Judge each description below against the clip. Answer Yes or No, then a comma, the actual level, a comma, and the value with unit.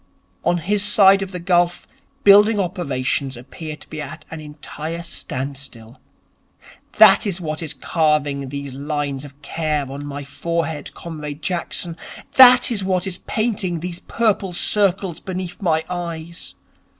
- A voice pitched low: No, medium, 170 Hz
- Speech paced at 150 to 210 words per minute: No, average, 140 wpm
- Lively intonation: No, average, 4.3 semitones